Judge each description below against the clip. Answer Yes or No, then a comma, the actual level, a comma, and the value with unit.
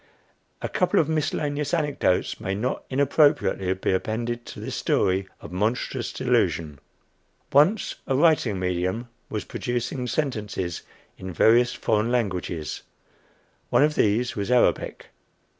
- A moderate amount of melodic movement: No, wide, 6.9 semitones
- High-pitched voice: No, low, 120 Hz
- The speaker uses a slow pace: Yes, slow, 125 wpm